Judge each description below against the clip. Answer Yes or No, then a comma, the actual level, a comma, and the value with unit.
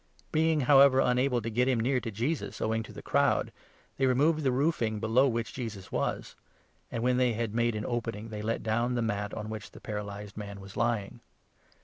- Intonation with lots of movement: No, average, 3.0 semitones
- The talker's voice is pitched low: Yes, low, 115 Hz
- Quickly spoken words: Yes, fast, 210 wpm